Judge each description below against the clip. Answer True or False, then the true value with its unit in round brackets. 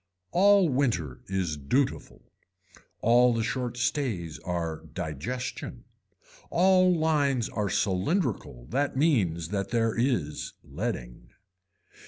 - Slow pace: True (100 wpm)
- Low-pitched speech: True (115 Hz)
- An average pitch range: False (8.5 semitones)